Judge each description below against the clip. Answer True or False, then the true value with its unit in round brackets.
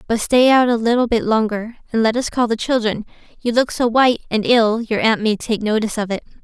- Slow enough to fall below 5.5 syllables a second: False (5.9 syllables/s)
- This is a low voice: False (225 Hz)